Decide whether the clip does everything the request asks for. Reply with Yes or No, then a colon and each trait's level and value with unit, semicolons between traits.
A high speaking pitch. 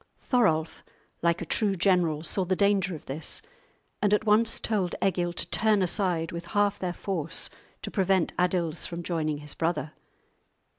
No: medium, 180 Hz